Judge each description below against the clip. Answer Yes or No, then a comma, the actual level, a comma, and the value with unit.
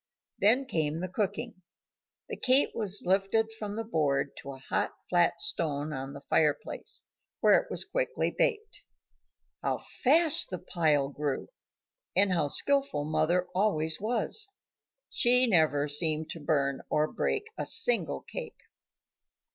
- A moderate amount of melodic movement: No, wide, 7.2 semitones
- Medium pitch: Yes, medium, 180 Hz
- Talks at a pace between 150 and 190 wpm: No, average, 140 wpm